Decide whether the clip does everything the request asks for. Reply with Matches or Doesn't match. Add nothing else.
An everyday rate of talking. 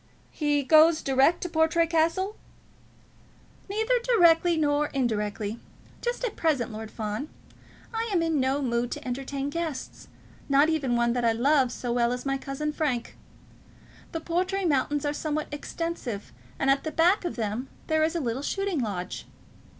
Matches